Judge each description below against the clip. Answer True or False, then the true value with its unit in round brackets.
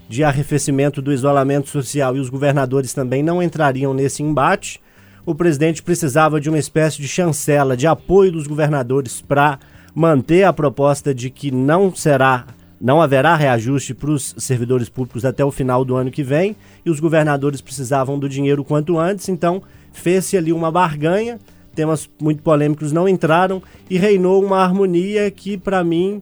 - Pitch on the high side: False (150 Hz)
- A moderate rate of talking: True (165 wpm)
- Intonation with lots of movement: False (3.8 semitones)